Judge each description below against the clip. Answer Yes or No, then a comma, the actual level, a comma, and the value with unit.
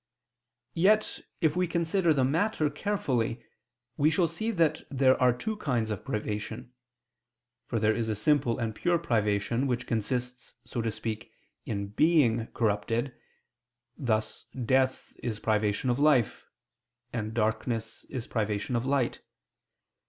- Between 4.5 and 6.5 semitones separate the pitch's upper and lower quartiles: Yes, average, 5.1 semitones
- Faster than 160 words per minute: No, slow, 135 wpm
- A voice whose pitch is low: Yes, low, 120 Hz